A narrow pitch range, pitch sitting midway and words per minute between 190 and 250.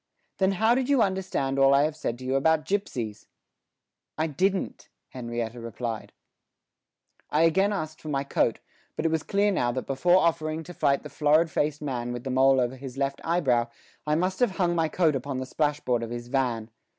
No: average, 4.9 semitones; medium, 145 Hz; average, 195 wpm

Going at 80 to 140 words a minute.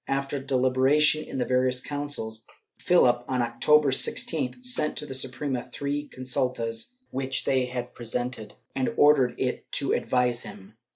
No: average, 150 wpm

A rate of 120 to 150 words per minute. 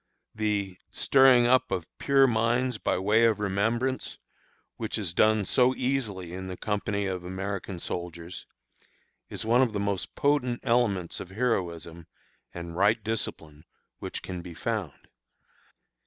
Yes: average, 140 wpm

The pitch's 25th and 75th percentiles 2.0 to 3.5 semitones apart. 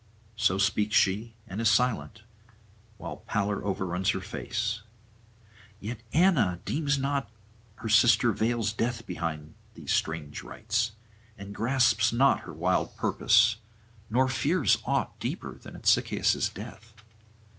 Yes: average, 3.2 semitones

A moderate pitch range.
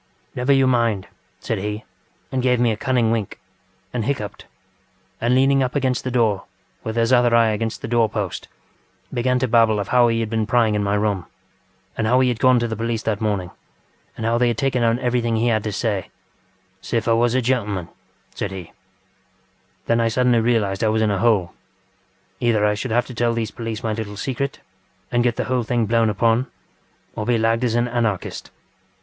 No: narrow, 2.3 semitones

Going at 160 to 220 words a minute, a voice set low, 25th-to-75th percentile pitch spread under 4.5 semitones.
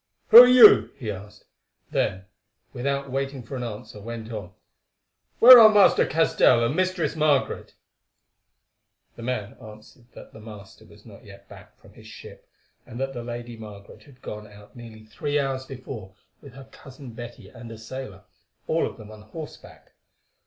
Yes: average, 165 wpm; low, 120 Hz; average, 4.1 semitones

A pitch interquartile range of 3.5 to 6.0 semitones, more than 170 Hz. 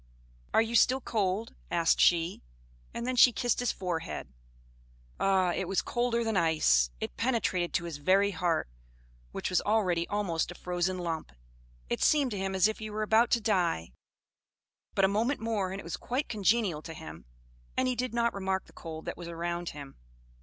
Yes: average, 4.8 semitones; high, 190 Hz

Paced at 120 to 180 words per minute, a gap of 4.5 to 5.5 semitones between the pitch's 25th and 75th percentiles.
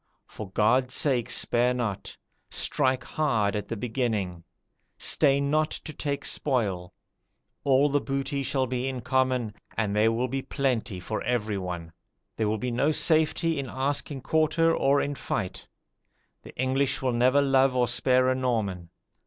No: average, 155 wpm; average, 3.8 semitones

